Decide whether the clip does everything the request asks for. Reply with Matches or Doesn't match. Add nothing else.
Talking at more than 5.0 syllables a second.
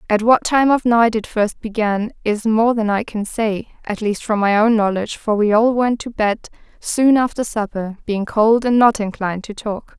Doesn't match